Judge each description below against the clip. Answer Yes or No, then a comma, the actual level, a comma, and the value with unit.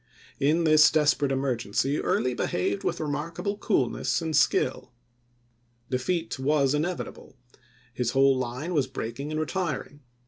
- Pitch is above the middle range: No, medium, 145 Hz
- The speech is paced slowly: Yes, slow, 130 wpm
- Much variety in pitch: No, average, 3.3 semitones